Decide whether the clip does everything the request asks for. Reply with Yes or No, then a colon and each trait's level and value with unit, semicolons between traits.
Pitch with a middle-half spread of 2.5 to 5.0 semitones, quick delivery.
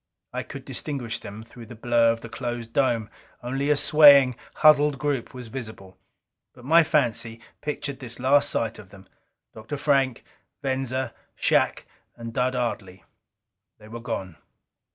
No: average, 3.3 semitones; average, 150 wpm